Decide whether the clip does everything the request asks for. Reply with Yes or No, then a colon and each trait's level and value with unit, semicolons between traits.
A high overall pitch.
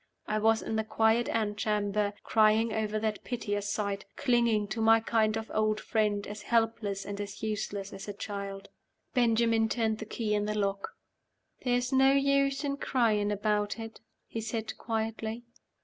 Yes: high, 220 Hz